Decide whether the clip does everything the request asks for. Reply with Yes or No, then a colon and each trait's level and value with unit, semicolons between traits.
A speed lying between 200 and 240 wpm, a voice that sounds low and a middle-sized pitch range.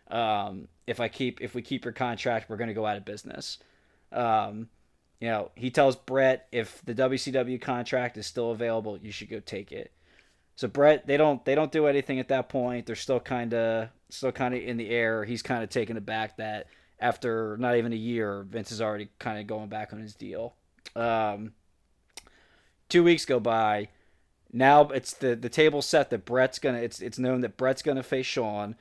Yes: fast, 205 wpm; low, 120 Hz; average, 3.1 semitones